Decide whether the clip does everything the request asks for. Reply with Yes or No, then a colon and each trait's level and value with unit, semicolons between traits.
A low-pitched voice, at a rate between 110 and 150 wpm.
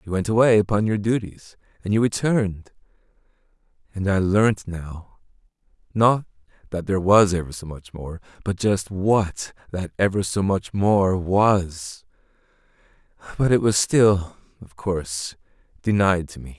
Yes: very low, 95 Hz; average, 140 wpm